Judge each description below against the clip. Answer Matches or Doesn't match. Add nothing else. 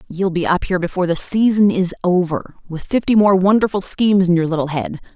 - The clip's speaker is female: Matches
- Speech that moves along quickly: Matches